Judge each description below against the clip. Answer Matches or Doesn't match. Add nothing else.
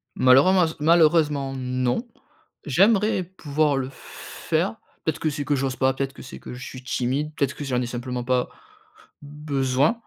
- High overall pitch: Doesn't match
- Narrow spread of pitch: Doesn't match